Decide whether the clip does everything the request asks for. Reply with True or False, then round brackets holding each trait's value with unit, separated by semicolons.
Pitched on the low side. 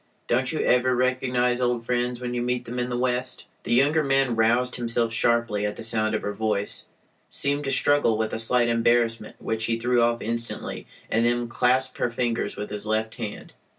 True (120 Hz)